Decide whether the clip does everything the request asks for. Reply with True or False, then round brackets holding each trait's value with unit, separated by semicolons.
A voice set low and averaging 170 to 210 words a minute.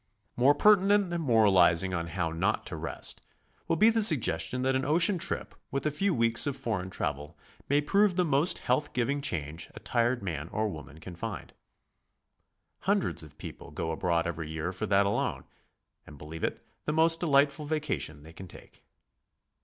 True (115 Hz; 175 wpm)